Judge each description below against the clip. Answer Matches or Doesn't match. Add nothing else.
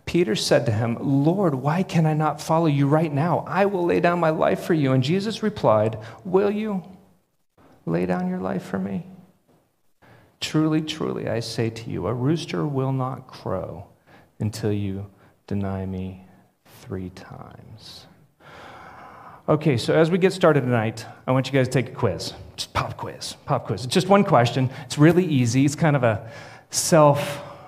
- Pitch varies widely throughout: Matches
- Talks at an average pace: Matches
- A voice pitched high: Doesn't match